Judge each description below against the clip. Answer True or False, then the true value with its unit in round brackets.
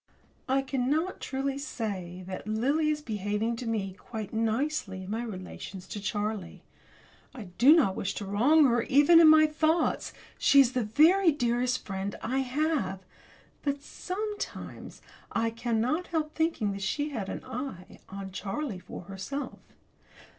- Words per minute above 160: False (150 wpm)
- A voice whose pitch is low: False (240 Hz)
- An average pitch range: False (6.6 semitones)